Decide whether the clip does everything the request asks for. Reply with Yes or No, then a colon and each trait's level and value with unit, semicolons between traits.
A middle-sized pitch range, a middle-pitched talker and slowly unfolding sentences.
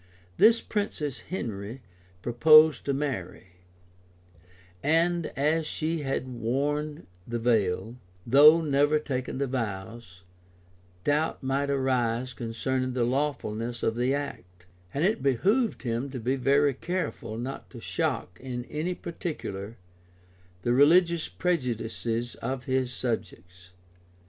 No: average, 4.2 semitones; low, 130 Hz; slow, 115 wpm